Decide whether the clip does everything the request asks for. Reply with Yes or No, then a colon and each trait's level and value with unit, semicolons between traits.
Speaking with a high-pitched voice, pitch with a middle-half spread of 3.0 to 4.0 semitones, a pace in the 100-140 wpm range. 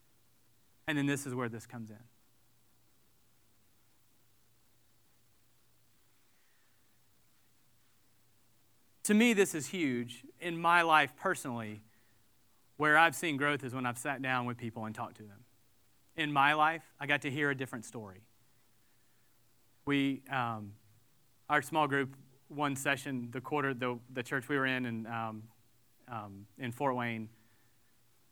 No: low, 120 Hz; average, 3.5 semitones; slow, 135 wpm